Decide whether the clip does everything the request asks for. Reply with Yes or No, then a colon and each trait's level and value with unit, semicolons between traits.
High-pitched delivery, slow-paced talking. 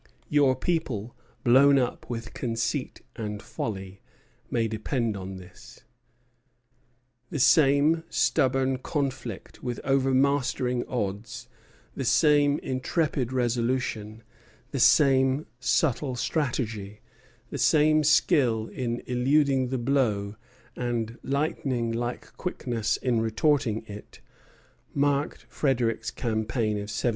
No: low, 125 Hz; slow, 100 wpm